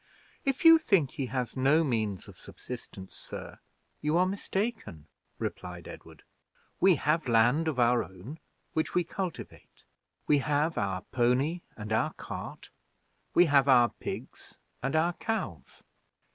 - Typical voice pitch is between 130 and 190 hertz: Yes, medium, 140 Hz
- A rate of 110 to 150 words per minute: Yes, average, 140 wpm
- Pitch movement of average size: No, wide, 6.3 semitones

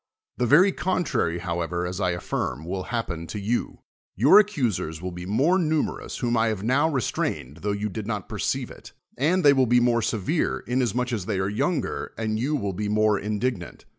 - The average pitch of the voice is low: Yes, low, 110 Hz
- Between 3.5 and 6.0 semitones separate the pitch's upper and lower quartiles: Yes, wide, 5.6 semitones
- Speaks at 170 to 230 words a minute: Yes, average, 195 wpm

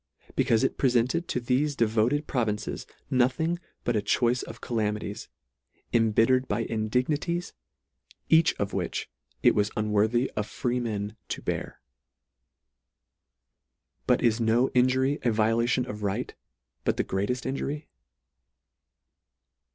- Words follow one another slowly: Yes, slow, 120 wpm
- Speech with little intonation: No, average, 3.2 semitones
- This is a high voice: No, low, 120 Hz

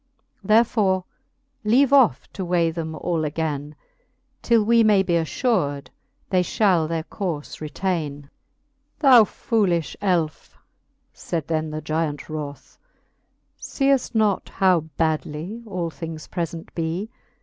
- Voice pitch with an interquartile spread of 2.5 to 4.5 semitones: No, average, 4.9 semitones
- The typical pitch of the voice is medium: Yes, medium, 170 Hz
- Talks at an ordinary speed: No, slow, 120 wpm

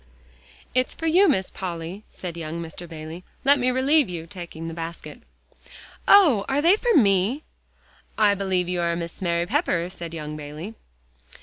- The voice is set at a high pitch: No, medium, 180 Hz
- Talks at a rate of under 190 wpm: Yes, average, 175 wpm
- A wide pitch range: Yes, wide, 7.1 semitones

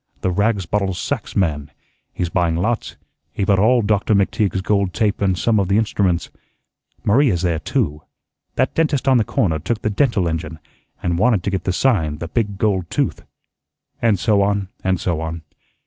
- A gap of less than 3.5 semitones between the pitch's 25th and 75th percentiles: No, average, 3.8 semitones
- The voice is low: Yes, low, 100 Hz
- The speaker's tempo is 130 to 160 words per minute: No, average, 180 wpm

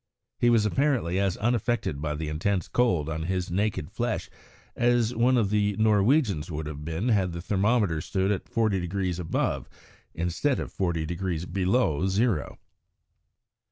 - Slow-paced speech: No, average, 155 wpm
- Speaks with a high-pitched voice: No, very low, 95 Hz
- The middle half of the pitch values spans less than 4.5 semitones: No, average, 4.9 semitones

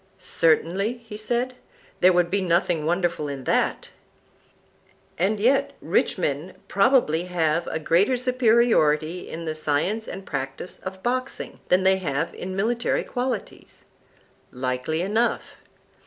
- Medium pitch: Yes, medium, 180 Hz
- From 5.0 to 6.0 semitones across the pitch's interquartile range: Yes, wide, 5.5 semitones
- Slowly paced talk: Yes, slow, 125 wpm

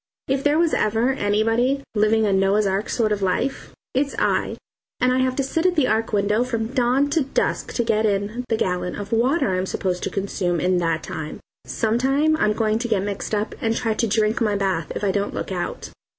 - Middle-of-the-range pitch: No, high, 220 Hz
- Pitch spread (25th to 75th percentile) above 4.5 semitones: No, average, 4.1 semitones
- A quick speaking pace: Yes, fast, 220 wpm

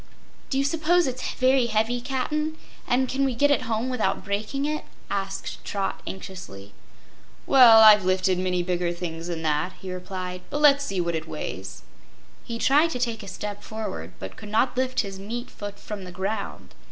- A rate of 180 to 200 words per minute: Yes, average, 185 wpm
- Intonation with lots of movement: Yes, wide, 5.9 semitones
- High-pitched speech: Yes, high, 210 Hz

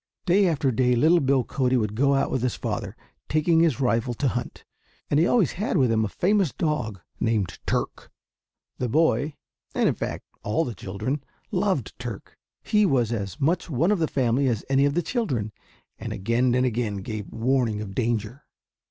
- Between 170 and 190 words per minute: Yes, average, 185 wpm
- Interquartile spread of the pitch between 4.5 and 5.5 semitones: Yes, average, 5.2 semitones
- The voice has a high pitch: No, low, 130 Hz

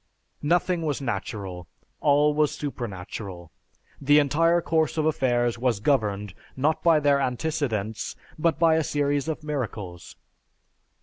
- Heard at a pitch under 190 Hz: Yes, medium, 140 Hz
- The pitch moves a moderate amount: No, wide, 6.0 semitones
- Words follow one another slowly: Yes, slow, 125 wpm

